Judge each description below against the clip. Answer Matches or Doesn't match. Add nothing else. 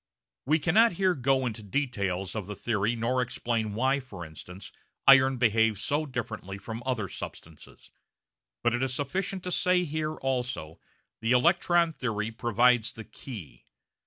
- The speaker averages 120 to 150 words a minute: Doesn't match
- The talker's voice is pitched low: Matches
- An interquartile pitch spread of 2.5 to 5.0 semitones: Matches